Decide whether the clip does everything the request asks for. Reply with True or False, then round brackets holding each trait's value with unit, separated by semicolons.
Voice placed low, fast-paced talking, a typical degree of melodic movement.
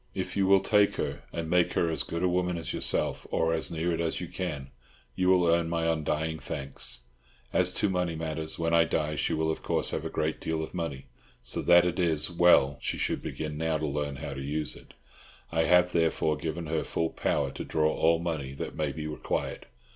False (80 Hz; 225 wpm; 1.8 semitones)